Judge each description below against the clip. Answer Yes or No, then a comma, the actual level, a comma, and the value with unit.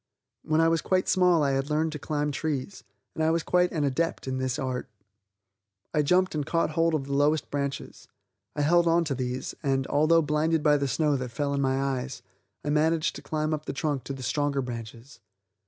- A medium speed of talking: No, fast, 210 wpm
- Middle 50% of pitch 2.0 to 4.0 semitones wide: Yes, average, 2.9 semitones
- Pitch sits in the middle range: Yes, medium, 145 Hz